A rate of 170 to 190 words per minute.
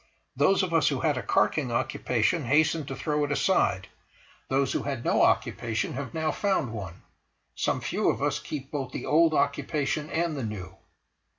Yes: average, 180 wpm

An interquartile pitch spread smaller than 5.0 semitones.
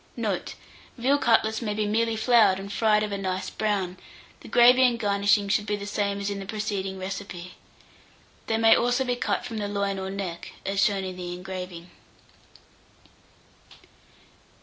Yes: narrow, 2.5 semitones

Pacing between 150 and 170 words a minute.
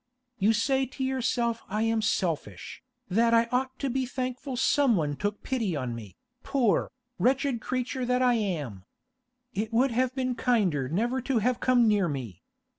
Yes: average, 165 wpm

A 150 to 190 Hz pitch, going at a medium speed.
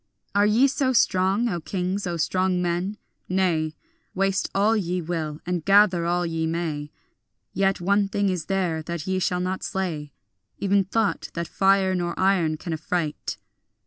Yes: medium, 185 Hz; average, 160 wpm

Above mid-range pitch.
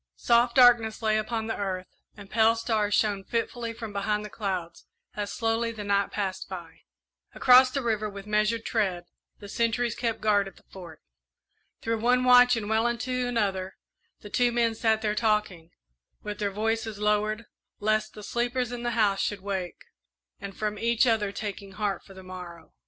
Yes: high, 215 Hz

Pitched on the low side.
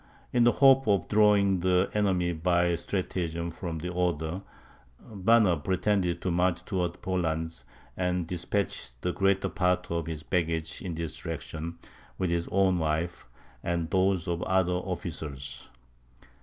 Yes: very low, 90 Hz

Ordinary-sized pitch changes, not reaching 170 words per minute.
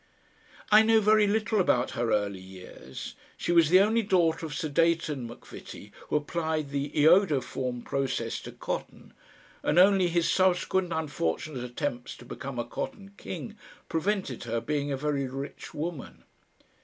No: wide, 6.0 semitones; average, 150 wpm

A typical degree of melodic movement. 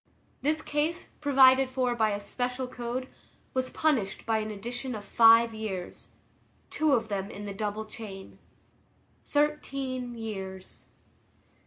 Yes: average, 3.7 semitones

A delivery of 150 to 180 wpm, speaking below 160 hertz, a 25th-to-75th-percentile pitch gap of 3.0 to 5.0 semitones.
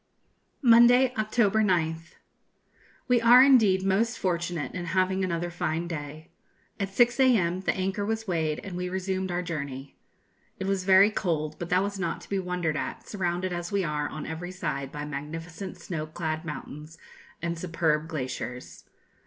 No: average, 160 wpm; medium, 175 Hz; average, 3.5 semitones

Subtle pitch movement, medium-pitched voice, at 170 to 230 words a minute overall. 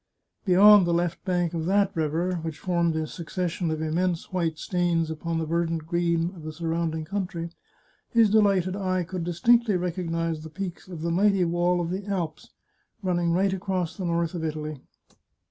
Yes: narrow, 2.1 semitones; medium, 175 Hz; average, 175 wpm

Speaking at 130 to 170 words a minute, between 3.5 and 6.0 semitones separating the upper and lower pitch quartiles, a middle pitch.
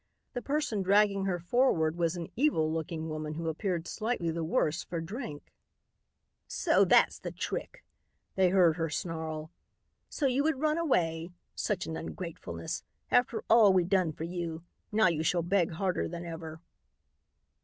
Yes: average, 155 wpm; average, 4.3 semitones; medium, 175 Hz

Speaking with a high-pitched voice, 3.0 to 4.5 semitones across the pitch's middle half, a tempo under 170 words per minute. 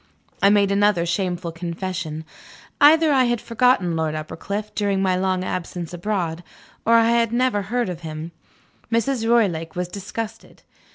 No: high, 195 Hz; average, 4.9 semitones; average, 150 wpm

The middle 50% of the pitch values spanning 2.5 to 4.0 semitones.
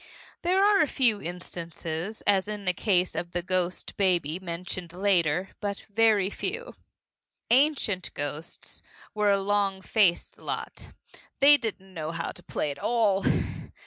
Yes: average, 3.6 semitones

